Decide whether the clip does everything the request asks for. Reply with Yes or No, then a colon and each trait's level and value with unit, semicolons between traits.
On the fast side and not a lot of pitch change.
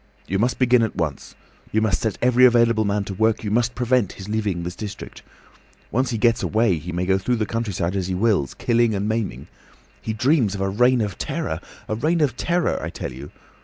No: fast, 220 wpm; average, 3.6 semitones